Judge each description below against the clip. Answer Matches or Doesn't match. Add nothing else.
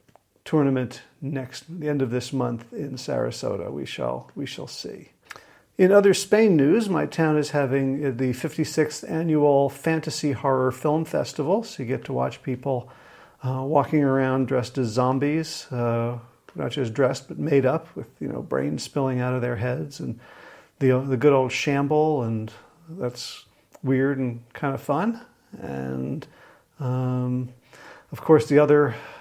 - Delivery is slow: Doesn't match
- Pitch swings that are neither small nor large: Matches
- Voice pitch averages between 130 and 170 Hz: Matches